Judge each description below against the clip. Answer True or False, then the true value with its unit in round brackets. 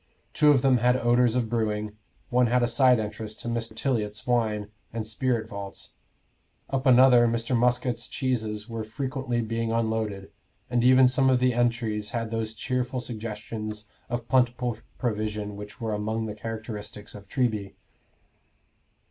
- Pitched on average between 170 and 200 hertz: False (115 Hz)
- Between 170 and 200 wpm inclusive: False (150 wpm)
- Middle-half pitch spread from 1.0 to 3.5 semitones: True (2.5 semitones)